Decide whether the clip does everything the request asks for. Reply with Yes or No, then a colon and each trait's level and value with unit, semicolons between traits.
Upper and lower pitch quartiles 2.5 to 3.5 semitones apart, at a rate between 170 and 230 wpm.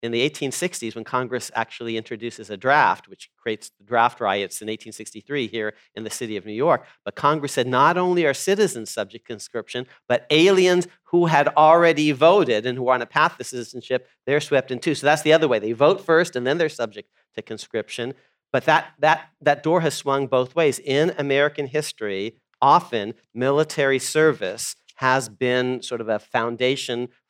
No: average, 4.5 semitones; average, 190 wpm